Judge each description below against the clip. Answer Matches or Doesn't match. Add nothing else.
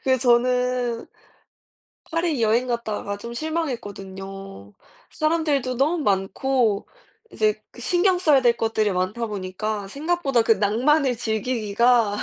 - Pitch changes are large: Doesn't match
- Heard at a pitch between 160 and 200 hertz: Doesn't match